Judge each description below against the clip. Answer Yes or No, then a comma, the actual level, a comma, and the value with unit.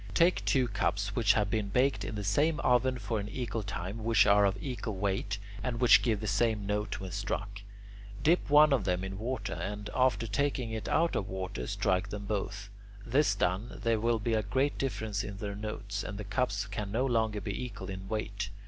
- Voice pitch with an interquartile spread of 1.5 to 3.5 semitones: Yes, average, 3.2 semitones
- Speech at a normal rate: No, fast, 210 wpm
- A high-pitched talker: No, low, 105 Hz